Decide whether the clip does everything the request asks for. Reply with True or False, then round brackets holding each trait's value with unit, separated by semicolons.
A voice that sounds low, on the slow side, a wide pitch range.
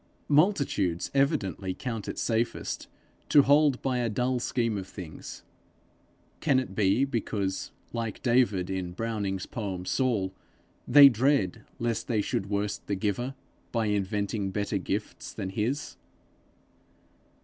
False (110 Hz; 125 wpm; 4.5 semitones)